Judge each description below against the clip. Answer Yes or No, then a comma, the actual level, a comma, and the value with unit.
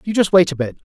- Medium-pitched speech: Yes, medium, 175 Hz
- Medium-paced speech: No, fast, 335 wpm